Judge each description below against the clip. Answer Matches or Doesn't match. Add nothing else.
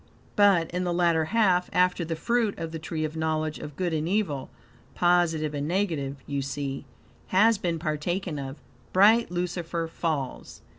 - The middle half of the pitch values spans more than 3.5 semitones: Doesn't match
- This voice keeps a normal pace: Matches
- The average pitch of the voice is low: Doesn't match